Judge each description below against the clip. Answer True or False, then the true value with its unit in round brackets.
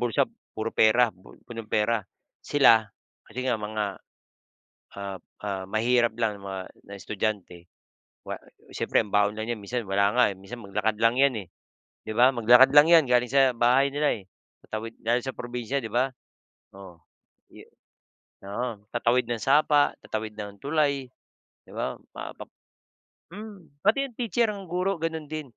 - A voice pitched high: False (120 Hz)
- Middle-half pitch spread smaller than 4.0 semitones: False (4.5 semitones)